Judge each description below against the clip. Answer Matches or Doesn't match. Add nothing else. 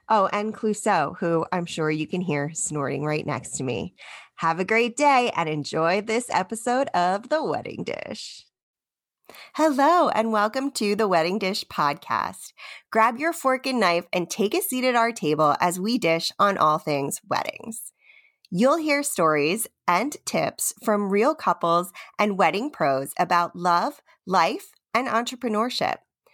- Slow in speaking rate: Doesn't match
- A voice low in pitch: Doesn't match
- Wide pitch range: Matches